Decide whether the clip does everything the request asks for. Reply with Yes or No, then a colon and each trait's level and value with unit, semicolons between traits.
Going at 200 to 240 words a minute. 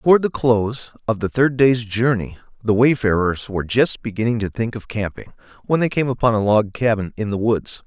Yes: fast, 205 wpm